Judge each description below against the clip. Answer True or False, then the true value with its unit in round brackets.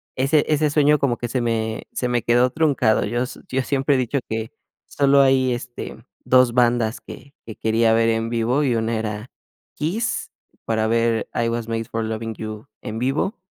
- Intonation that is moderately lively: True (3.1 semitones)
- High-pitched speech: False (120 Hz)